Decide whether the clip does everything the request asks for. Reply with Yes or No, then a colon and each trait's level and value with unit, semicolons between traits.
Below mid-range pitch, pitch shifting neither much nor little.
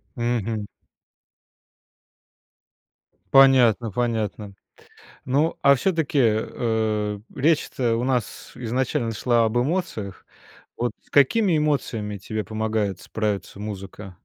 Yes: low, 115 Hz; average, 3.8 semitones